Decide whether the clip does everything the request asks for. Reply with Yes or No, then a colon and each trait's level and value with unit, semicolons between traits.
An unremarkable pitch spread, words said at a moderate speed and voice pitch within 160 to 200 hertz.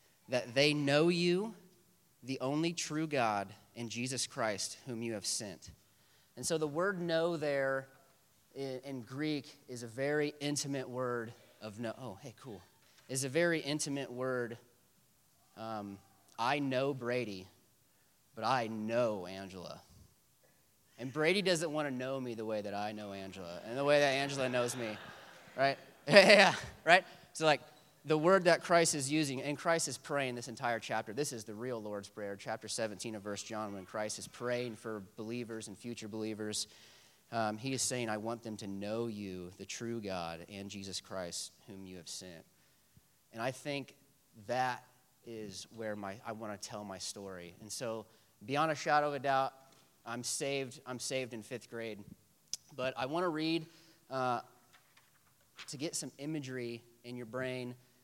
No: average, 4.7 semitones; average, 170 wpm; low, 125 Hz